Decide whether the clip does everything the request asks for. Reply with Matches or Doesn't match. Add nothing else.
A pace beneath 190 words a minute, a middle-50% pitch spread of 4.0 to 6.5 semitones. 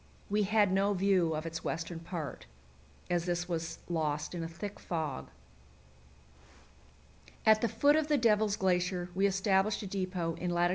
Doesn't match